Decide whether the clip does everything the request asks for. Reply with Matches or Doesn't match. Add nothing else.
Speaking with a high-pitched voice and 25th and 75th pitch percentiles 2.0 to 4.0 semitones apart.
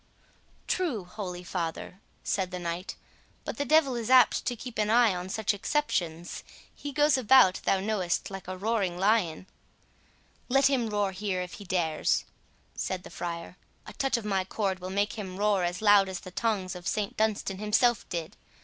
Matches